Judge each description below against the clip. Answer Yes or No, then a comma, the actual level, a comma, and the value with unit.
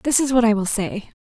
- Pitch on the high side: Yes, high, 230 Hz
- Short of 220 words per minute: No, fast, 295 wpm